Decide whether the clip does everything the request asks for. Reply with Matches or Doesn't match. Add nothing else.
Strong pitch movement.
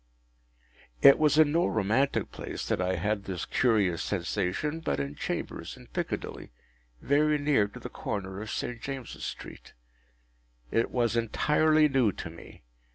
Matches